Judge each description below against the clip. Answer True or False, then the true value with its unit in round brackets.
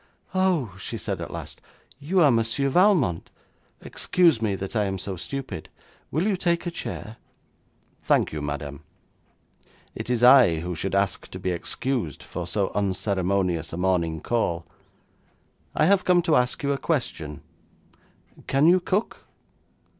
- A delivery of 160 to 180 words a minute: False (150 wpm)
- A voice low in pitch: True (115 Hz)